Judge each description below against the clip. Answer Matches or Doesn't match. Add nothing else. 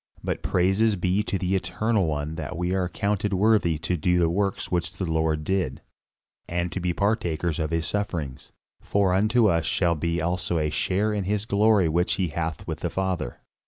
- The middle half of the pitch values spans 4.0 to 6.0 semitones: Doesn't match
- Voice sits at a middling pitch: Doesn't match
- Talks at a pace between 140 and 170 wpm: Doesn't match